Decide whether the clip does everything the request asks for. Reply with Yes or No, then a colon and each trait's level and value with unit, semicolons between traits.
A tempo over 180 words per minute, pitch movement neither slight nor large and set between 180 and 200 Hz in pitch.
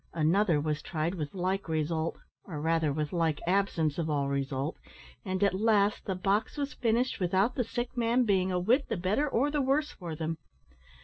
No: average, 190 wpm; wide, 5.9 semitones; medium, 185 Hz